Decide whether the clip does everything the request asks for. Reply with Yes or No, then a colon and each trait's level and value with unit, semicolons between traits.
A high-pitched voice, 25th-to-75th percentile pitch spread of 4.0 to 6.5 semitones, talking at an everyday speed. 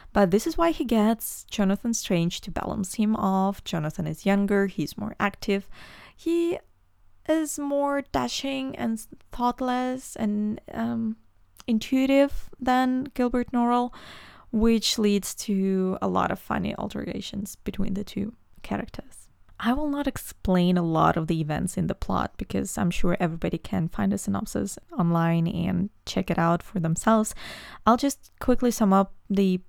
Yes: high, 210 Hz; average, 4.6 semitones; average, 150 wpm